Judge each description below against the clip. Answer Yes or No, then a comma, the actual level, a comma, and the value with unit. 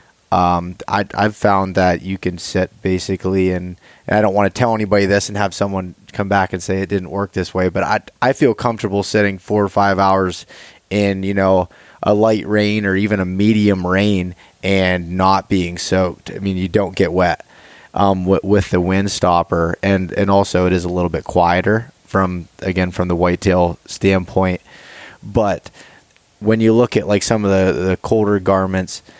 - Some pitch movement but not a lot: No, narrow, 1.9 semitones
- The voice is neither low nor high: No, very low, 95 Hz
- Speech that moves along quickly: No, average, 195 wpm